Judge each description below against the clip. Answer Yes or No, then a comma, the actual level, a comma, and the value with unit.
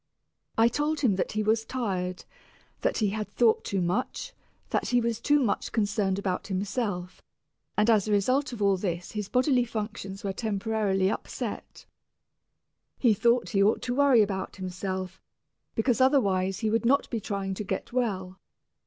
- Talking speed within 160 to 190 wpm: Yes, average, 170 wpm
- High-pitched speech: Yes, high, 210 Hz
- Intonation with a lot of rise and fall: No, average, 3.7 semitones